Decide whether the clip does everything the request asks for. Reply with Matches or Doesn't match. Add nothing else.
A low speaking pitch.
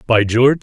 Matches